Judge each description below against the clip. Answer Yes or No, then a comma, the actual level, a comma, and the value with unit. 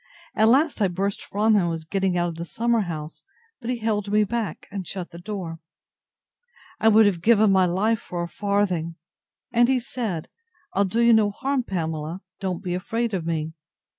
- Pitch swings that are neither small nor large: Yes, average, 4.4 semitones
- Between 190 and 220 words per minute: Yes, average, 195 wpm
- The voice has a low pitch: No, high, 200 Hz